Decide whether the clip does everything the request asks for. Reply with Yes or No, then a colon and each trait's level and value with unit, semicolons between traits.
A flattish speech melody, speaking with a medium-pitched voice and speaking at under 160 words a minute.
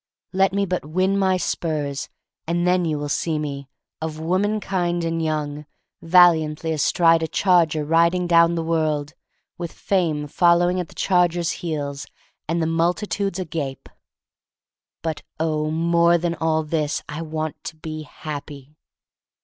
Yes: narrow, 2.2 semitones; medium, 165 Hz; average, 150 wpm